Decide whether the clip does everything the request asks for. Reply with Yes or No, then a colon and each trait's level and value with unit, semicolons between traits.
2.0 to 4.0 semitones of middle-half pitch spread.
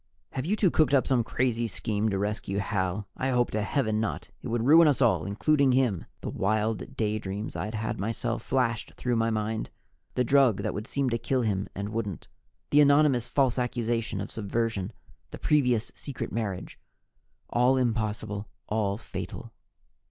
Yes: average, 3.4 semitones